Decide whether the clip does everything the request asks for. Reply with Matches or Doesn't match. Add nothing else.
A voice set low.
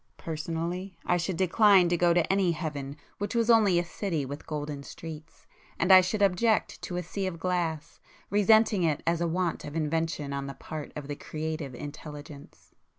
Doesn't match